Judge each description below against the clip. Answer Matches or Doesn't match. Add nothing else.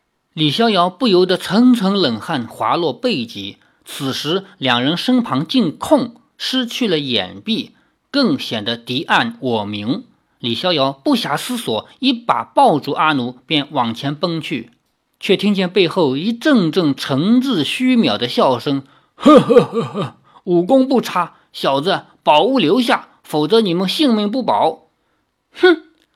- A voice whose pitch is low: Doesn't match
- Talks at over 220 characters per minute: Doesn't match